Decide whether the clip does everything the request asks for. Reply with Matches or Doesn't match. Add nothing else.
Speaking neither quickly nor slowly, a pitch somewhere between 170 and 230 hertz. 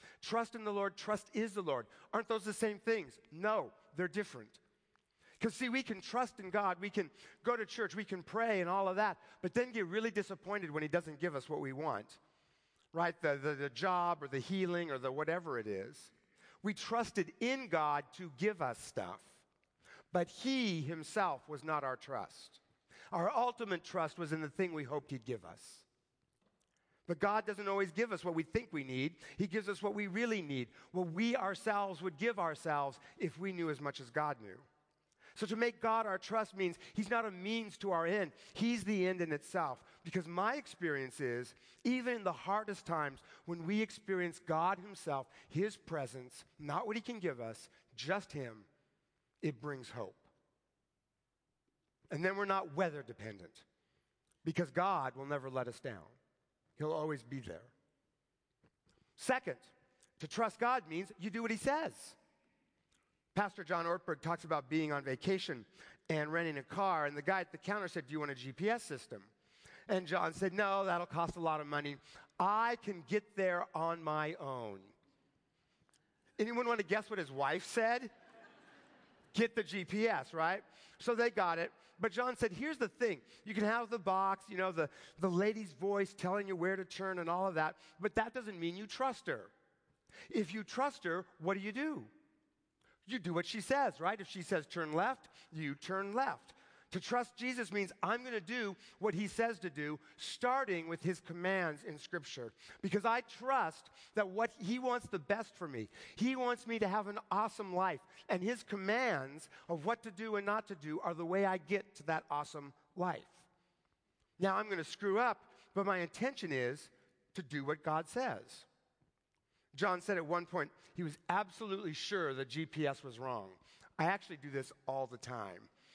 Matches